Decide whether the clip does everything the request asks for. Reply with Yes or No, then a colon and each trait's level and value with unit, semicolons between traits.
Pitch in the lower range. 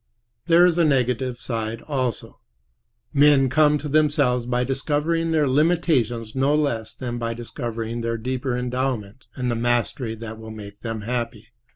Yes: low, 125 Hz